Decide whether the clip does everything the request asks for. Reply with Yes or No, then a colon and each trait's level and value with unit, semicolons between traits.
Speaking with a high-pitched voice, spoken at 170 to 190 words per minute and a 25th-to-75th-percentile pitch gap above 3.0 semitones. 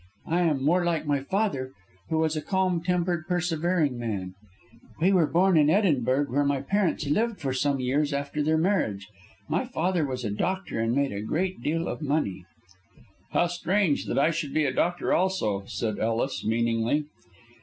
No: medium, 150 Hz; average, 175 wpm; average, 5.3 semitones